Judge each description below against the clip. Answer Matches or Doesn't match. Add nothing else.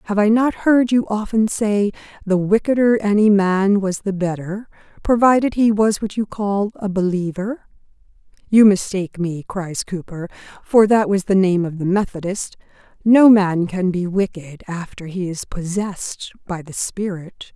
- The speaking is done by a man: Doesn't match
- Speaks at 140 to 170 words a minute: Matches